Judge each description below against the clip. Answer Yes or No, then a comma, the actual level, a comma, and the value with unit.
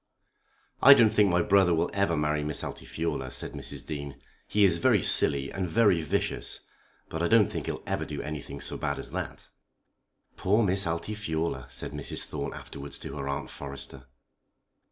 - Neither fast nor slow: Yes, average, 175 wpm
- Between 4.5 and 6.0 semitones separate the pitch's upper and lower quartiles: Yes, wide, 5.5 semitones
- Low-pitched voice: Yes, very low, 80 Hz